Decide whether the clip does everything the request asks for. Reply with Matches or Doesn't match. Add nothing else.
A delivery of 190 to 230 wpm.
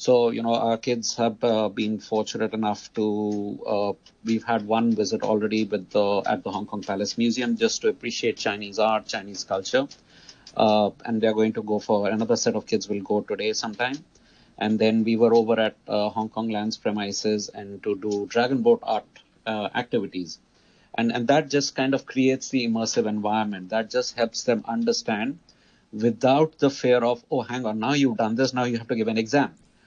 Matches